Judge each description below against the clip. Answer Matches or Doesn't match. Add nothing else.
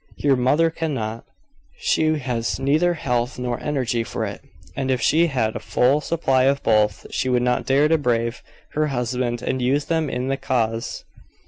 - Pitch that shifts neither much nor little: Matches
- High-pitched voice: Doesn't match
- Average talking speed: Matches